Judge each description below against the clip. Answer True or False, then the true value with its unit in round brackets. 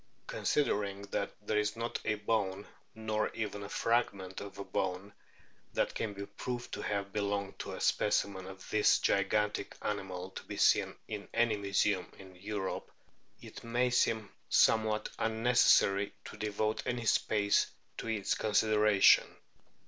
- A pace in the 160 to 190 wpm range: False (150 wpm)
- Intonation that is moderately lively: False (1.9 semitones)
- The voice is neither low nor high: False (105 Hz)